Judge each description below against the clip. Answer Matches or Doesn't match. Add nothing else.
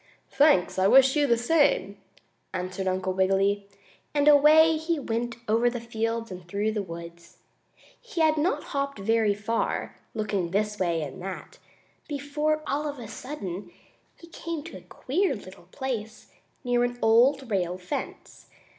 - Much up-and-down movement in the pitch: Matches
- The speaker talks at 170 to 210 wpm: Doesn't match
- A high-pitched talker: Matches